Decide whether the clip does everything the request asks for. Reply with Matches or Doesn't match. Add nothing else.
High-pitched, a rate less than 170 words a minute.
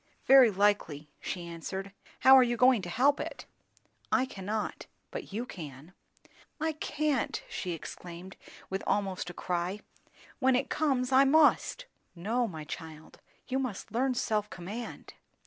Matches